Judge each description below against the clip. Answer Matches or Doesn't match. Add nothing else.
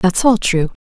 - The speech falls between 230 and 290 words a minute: Doesn't match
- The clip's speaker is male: Doesn't match